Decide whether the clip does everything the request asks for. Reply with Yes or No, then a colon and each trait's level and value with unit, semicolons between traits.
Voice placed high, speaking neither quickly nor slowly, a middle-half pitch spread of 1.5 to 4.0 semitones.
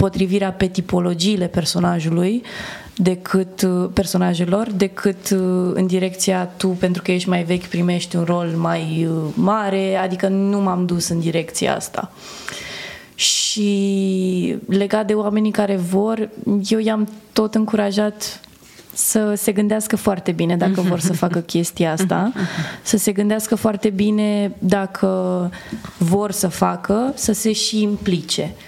Yes: high, 195 Hz; average, 130 wpm; average, 2.7 semitones